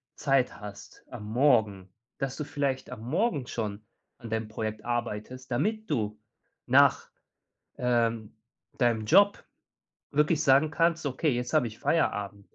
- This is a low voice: Yes, low, 120 Hz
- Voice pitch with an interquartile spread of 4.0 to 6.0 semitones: Yes, average, 5.1 semitones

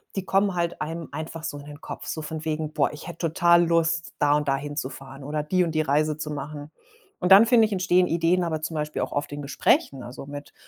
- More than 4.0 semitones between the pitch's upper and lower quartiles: No, average, 2.8 semitones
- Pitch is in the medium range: Yes, medium, 155 Hz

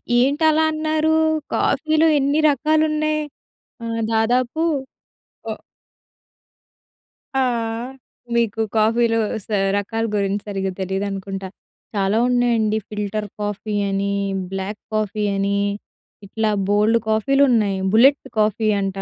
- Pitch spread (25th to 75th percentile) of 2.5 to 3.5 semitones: No, average, 5.2 semitones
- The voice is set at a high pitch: Yes, high, 220 Hz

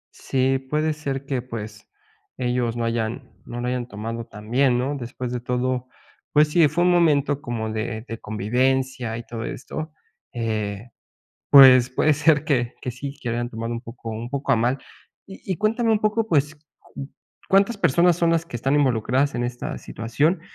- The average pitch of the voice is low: Yes, low, 130 Hz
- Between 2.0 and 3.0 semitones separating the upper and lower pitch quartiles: No, average, 3.9 semitones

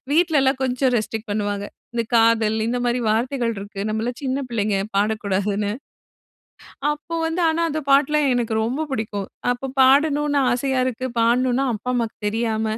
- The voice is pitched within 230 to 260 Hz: Yes, high, 240 Hz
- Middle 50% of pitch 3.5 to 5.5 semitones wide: Yes, average, 3.8 semitones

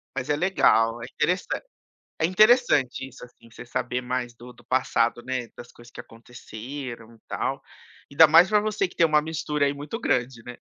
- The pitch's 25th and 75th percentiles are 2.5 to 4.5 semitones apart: No, average, 5.1 semitones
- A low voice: Yes, low, 130 Hz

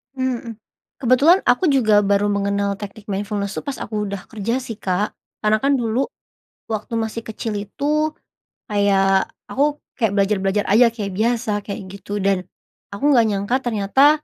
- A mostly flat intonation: No, average, 3.4 semitones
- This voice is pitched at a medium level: No, high, 215 Hz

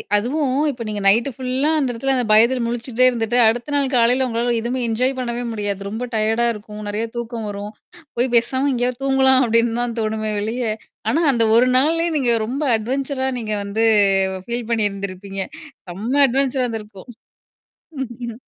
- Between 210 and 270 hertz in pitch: Yes, high, 235 Hz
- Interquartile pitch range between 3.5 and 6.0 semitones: No, average, 2.8 semitones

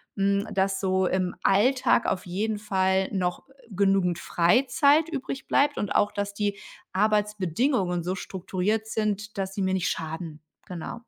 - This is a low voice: No, high, 195 Hz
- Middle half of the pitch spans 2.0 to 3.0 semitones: Yes, narrow, 2.5 semitones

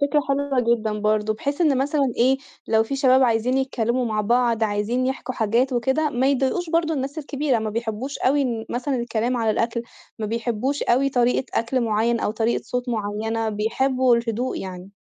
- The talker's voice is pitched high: Yes, high, 240 Hz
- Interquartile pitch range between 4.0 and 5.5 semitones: No, average, 3.1 semitones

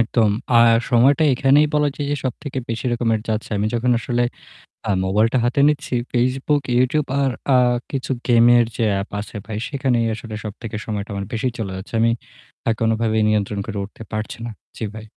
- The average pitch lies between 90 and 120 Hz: Yes, low, 115 Hz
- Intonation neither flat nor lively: Yes, average, 3.1 semitones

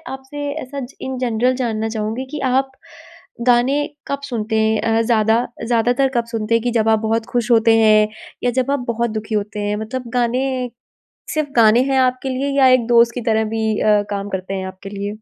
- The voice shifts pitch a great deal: No, average, 2.9 semitones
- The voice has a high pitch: Yes, high, 235 Hz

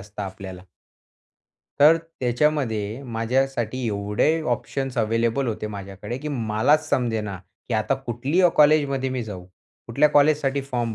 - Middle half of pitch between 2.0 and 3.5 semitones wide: No, average, 4.7 semitones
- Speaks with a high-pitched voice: No, low, 125 Hz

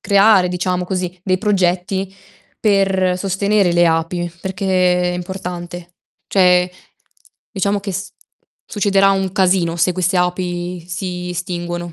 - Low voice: No, medium, 180 Hz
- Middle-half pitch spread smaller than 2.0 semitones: Yes, narrow, 1.5 semitones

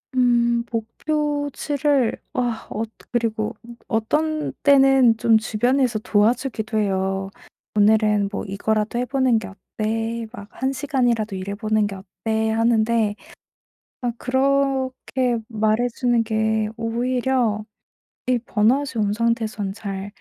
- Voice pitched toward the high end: Yes, high, 230 Hz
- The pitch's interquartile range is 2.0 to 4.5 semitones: Yes, average, 2.9 semitones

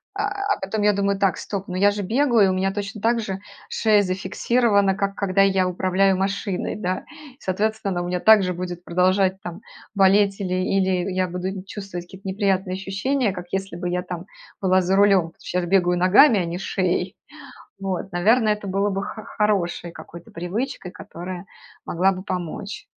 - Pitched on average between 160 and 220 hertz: Yes, high, 190 Hz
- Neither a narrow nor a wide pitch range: No, narrow, 1.8 semitones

